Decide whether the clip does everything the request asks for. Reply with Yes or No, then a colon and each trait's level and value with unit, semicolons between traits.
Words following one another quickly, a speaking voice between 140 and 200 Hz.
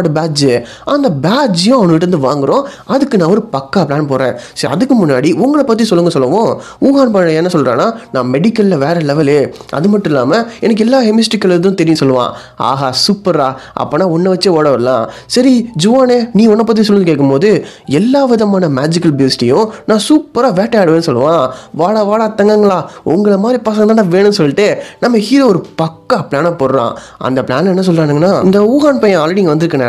Yes: fast, 160 wpm; high, 190 Hz